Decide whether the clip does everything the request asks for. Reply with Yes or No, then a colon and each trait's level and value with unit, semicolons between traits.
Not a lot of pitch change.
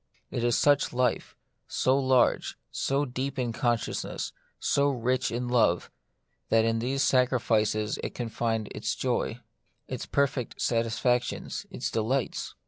Yes: narrow, 2.3 semitones